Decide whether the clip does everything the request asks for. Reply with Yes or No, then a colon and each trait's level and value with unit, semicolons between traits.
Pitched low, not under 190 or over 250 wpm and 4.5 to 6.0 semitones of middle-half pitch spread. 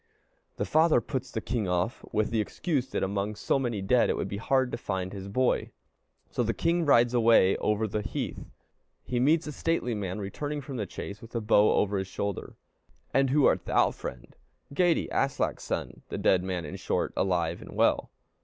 Yes: low, 110 Hz; average, 200 wpm; average, 5.1 semitones